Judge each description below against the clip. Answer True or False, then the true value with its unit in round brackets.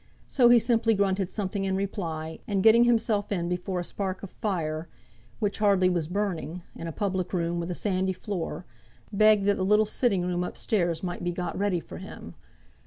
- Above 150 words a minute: True (195 wpm)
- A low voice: False (190 Hz)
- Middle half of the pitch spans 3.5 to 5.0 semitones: False (2.8 semitones)